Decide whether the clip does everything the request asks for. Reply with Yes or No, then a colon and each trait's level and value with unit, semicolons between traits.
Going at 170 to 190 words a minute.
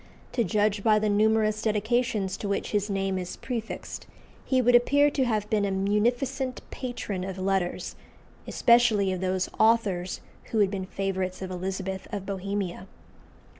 No: average, 155 wpm